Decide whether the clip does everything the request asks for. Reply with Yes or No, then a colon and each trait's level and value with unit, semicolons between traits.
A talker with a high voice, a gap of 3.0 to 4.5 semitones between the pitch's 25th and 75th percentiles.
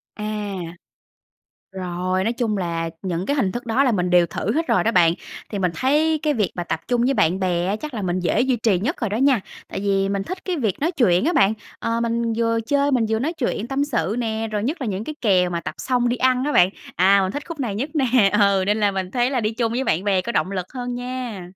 No: high, 220 Hz; average, 5.1 semitones